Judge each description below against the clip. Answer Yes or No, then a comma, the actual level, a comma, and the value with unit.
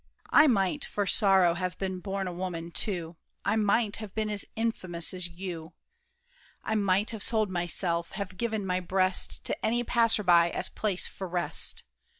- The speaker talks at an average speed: Yes, average, 170 wpm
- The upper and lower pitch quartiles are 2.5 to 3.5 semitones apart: Yes, average, 3.2 semitones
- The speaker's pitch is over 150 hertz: Yes, high, 190 Hz